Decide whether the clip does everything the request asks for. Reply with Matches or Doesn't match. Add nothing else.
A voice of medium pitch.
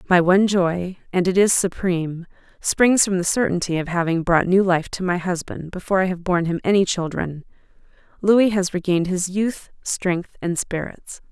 Matches